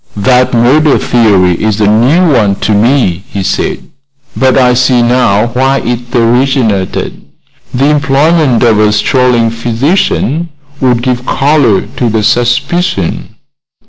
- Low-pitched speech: Yes, low, 125 Hz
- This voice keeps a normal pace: No, slow, 130 wpm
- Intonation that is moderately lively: Yes, average, 3.5 semitones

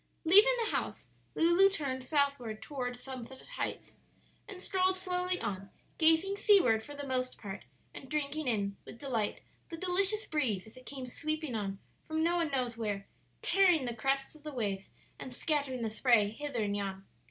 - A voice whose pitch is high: Yes, very high, 275 Hz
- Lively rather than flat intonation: Yes, wide, 6.2 semitones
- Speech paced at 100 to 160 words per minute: No, average, 175 wpm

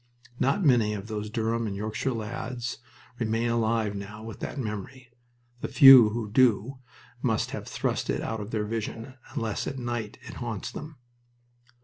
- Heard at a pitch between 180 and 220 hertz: No, low, 115 Hz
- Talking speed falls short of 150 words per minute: No, average, 160 wpm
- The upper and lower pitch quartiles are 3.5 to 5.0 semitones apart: No, narrow, 2.4 semitones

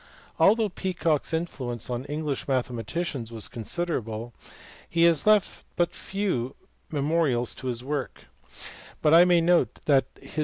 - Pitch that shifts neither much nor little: No, wide, 5.8 semitones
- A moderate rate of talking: Yes, average, 145 wpm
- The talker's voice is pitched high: No, medium, 150 Hz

